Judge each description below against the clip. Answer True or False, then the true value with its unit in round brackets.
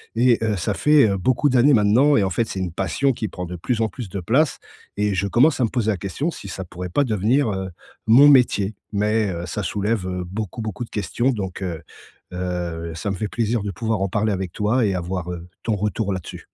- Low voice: True (105 Hz)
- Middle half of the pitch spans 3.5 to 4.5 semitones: True (4.0 semitones)